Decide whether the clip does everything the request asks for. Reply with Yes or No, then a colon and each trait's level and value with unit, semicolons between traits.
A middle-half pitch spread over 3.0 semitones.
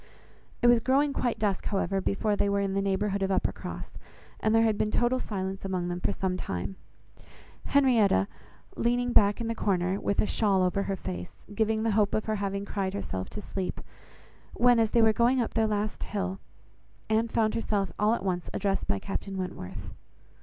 No: average, 2.7 semitones